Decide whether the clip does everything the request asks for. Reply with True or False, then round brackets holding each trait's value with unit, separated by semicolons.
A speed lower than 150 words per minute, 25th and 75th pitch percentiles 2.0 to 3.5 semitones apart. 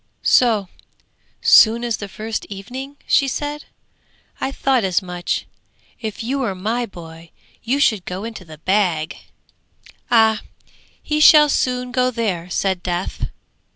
False (135 wpm; 5.3 semitones)